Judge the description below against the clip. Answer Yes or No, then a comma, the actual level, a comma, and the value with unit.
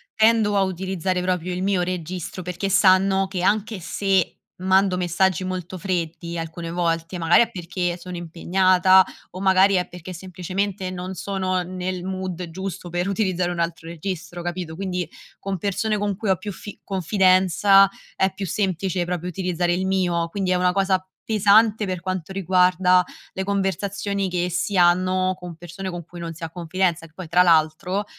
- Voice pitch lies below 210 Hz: Yes, medium, 185 Hz